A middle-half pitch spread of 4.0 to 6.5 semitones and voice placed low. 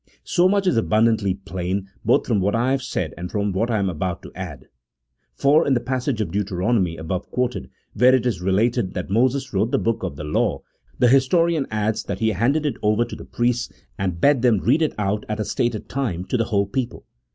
Yes: average, 4.6 semitones; low, 110 Hz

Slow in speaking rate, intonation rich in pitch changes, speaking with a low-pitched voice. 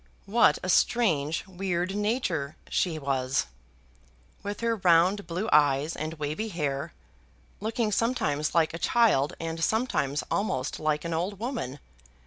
No: slow, 130 wpm; wide, 5.7 semitones; medium, 170 Hz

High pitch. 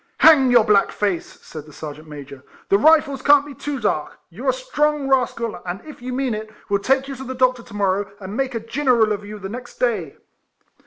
Yes: high, 240 Hz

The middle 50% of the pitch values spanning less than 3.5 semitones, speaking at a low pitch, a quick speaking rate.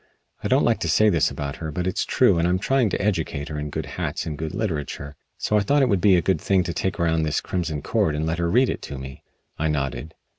No: average, 4.1 semitones; very low, 85 Hz; fast, 270 wpm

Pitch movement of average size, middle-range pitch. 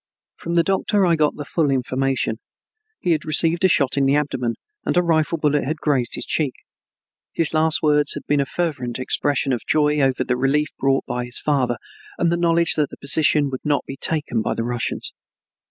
Yes: average, 3.1 semitones; medium, 145 Hz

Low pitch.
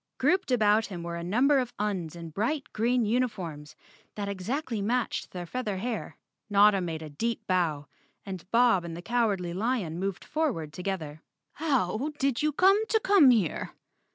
No: high, 210 Hz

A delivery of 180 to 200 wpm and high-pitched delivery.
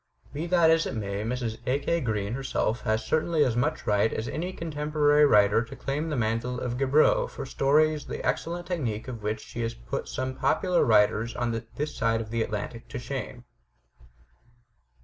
No: average, 185 wpm; low, 125 Hz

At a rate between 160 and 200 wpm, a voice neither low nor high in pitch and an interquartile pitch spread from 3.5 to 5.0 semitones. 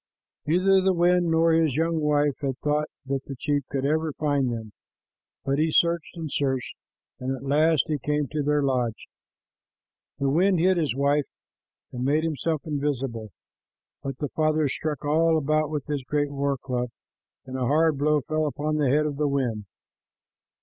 No: average, 175 wpm; medium, 150 Hz; narrow, 2.5 semitones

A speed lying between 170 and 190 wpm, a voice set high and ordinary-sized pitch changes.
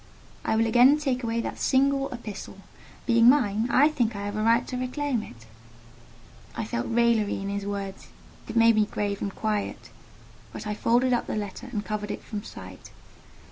Yes: average, 185 wpm; high, 230 Hz; average, 3.4 semitones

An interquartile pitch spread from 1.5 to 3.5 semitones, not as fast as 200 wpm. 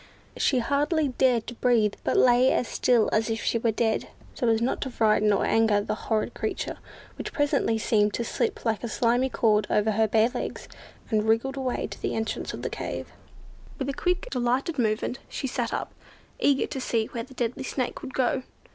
No: average, 2.9 semitones; fast, 205 wpm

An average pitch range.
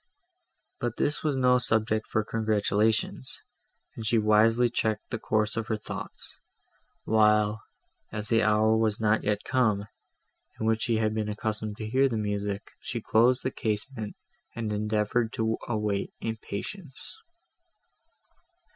No: narrow, 1.3 semitones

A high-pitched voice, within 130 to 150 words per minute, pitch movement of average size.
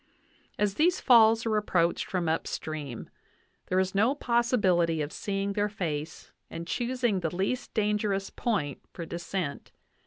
Yes: high, 195 Hz; average, 145 wpm; average, 4.8 semitones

